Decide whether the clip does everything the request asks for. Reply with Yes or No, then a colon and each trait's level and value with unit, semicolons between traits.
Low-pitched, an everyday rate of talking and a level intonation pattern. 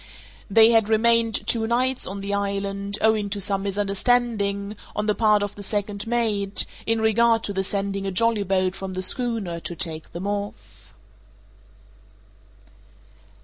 No: high, 205 Hz; average, 145 wpm; narrow, 2.2 semitones